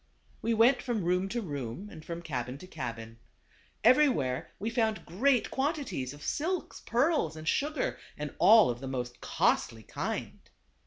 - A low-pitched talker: No, medium, 180 Hz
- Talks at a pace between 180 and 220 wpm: No, average, 155 wpm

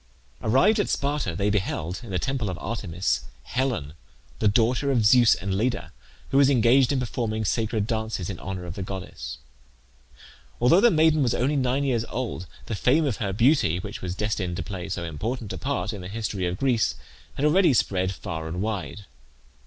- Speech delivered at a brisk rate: No, average, 190 wpm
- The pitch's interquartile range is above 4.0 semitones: Yes, wide, 5.6 semitones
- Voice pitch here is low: Yes, low, 110 Hz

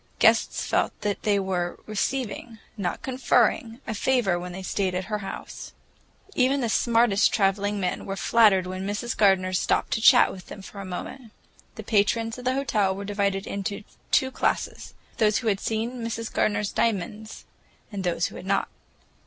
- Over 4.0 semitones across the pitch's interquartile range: No, average, 3.0 semitones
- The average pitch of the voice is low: No, high, 205 Hz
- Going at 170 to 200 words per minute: Yes, average, 175 wpm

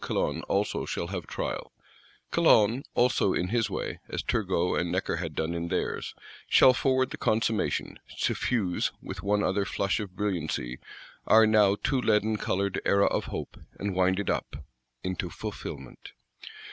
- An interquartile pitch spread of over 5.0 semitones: No, average, 3.3 semitones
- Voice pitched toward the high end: No, low, 100 Hz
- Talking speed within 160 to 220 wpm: No, average, 150 wpm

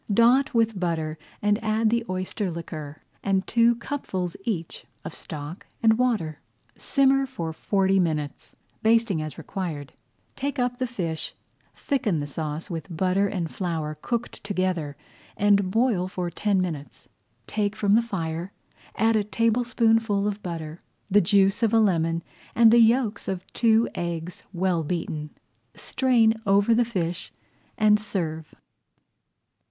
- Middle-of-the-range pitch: No, high, 195 Hz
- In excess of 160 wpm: No, average, 140 wpm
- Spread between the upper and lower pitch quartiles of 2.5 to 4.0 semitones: No, average, 5.2 semitones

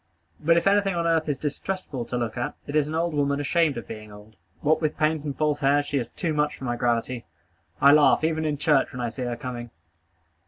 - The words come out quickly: Yes, fast, 240 wpm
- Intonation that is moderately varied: Yes, average, 4.3 semitones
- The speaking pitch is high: No, medium, 145 Hz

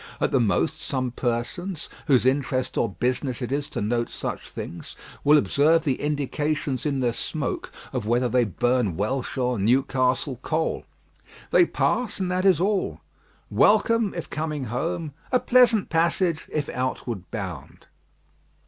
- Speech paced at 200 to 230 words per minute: No, average, 150 wpm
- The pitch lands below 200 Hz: Yes, low, 135 Hz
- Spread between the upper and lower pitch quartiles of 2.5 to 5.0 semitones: Yes, average, 4.7 semitones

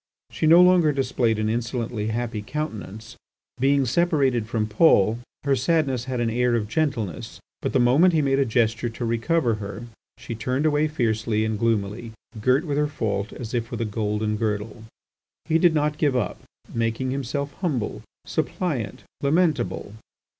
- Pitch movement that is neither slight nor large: Yes, average, 4.6 semitones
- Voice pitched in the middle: No, low, 120 Hz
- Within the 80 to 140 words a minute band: No, average, 160 wpm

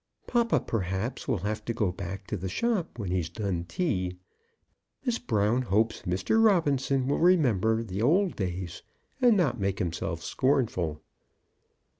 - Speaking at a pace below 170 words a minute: Yes, average, 140 wpm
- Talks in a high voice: No, low, 110 Hz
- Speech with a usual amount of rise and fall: No, wide, 7.6 semitones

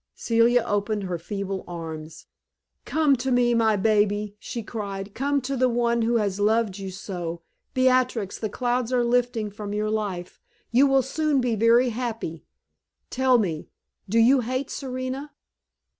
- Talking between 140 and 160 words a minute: Yes, average, 155 wpm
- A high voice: Yes, high, 230 Hz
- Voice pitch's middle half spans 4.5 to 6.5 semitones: No, average, 3.7 semitones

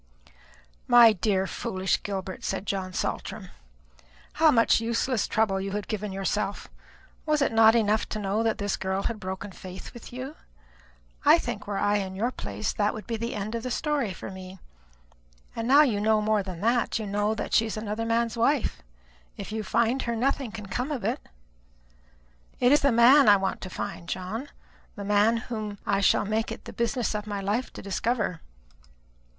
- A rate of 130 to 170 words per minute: No, average, 190 wpm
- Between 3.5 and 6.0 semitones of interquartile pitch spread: No, average, 3.0 semitones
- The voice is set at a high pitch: Yes, high, 215 Hz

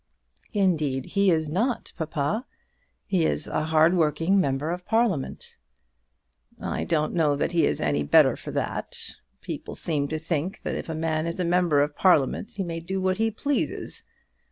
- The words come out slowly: No, average, 175 wpm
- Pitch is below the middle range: No, medium, 165 Hz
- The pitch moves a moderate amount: Yes, average, 3.7 semitones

